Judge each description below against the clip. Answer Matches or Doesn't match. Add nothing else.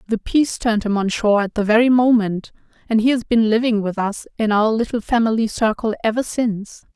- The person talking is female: Matches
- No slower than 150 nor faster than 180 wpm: Doesn't match